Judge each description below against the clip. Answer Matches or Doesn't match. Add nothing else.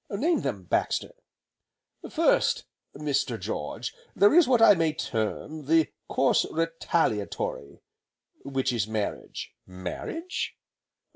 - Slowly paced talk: Matches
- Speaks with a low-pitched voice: Doesn't match